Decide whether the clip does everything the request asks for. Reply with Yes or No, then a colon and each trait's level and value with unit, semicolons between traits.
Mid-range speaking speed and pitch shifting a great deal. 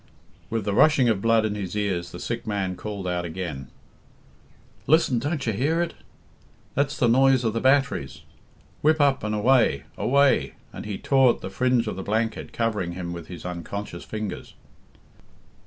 Yes: average, 170 wpm; wide, 5.9 semitones